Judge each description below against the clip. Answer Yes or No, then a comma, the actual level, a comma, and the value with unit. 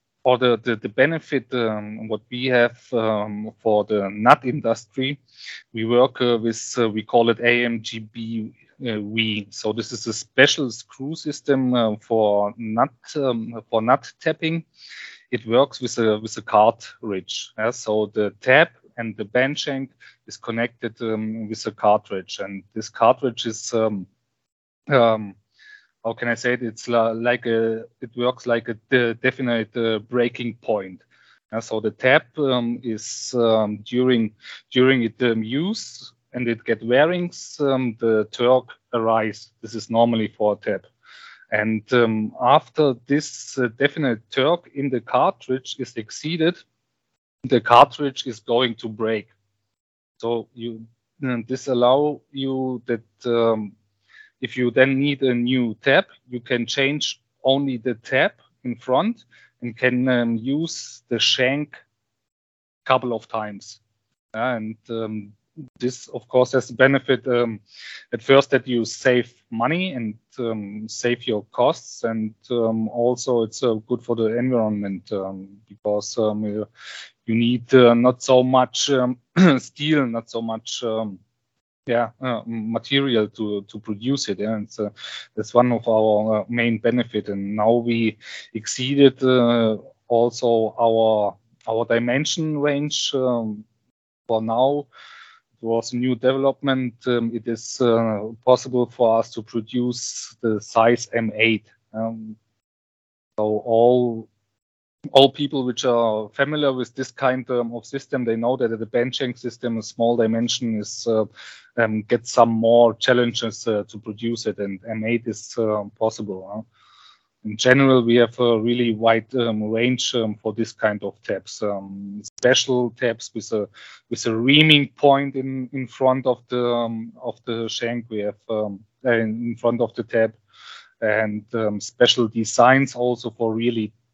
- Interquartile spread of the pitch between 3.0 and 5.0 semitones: No, narrow, 2.4 semitones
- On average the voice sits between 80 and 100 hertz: No, low, 115 Hz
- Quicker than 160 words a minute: No, average, 150 wpm